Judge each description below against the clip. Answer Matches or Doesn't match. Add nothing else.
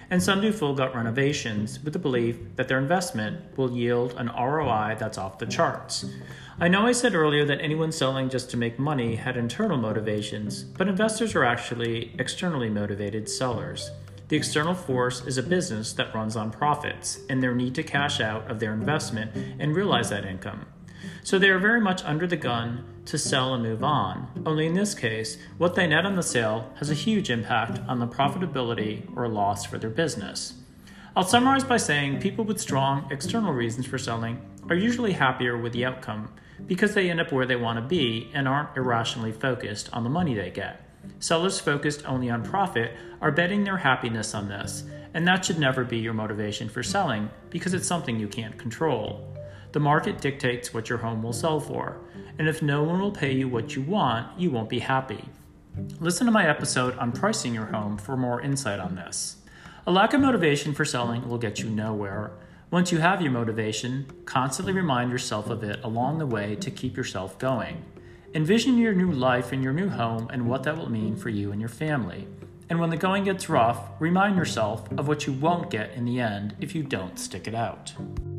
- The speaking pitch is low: Matches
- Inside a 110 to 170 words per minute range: Doesn't match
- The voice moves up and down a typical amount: Doesn't match